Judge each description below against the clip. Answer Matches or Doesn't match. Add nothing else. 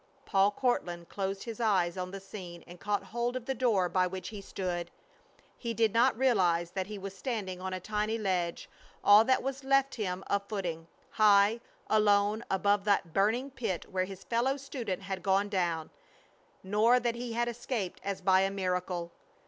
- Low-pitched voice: Doesn't match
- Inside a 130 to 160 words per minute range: Doesn't match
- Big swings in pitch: Doesn't match